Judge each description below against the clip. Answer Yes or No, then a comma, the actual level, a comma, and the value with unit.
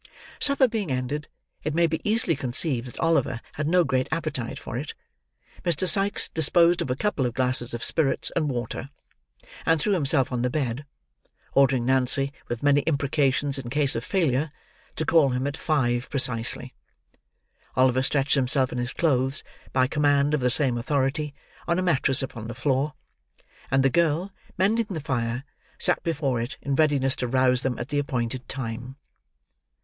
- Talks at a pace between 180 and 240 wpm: No, average, 165 wpm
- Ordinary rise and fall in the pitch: Yes, average, 3.5 semitones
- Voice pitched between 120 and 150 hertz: Yes, low, 135 Hz